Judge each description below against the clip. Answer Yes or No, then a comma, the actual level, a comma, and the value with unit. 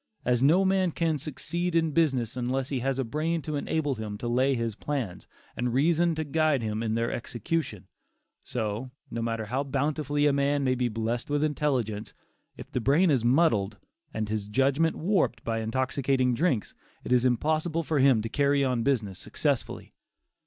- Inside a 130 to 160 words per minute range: No, average, 180 wpm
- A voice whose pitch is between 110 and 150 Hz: Yes, low, 135 Hz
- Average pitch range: Yes, average, 4.7 semitones